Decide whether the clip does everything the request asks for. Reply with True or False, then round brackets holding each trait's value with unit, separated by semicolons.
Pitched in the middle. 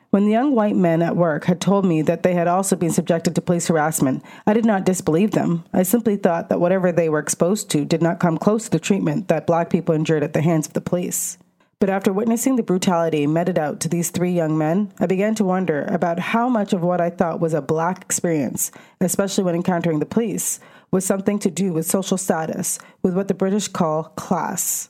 True (180 Hz)